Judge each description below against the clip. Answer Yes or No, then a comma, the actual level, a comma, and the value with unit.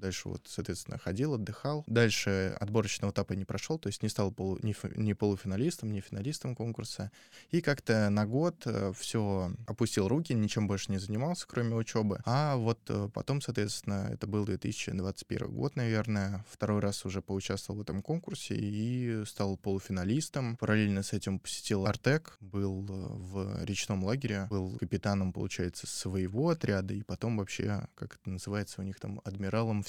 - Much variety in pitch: No, average, 3.0 semitones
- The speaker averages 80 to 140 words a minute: No, average, 155 wpm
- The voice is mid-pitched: No, low, 105 Hz